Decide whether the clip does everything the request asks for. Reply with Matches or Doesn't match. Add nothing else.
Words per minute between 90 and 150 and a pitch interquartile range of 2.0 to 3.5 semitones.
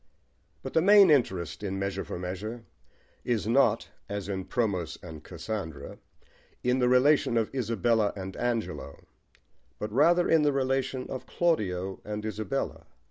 Doesn't match